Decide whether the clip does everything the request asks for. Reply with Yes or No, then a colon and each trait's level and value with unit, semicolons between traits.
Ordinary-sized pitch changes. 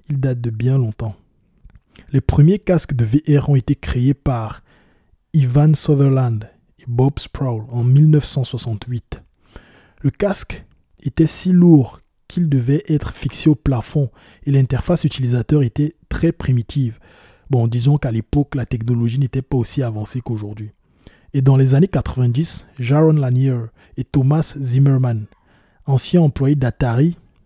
Yes: average, 3.8 semitones